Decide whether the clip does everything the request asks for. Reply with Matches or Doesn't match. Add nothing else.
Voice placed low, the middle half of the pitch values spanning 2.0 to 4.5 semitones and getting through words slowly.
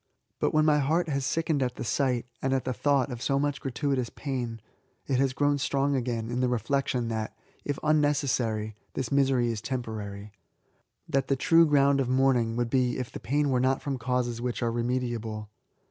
Doesn't match